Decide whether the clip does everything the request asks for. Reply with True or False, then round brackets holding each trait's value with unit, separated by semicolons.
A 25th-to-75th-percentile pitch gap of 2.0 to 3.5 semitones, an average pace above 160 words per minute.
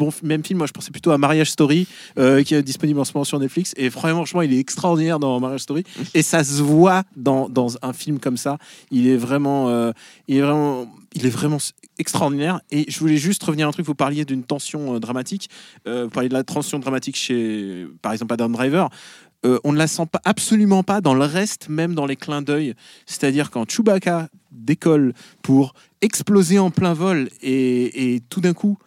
False (4.2 semitones; 215 wpm)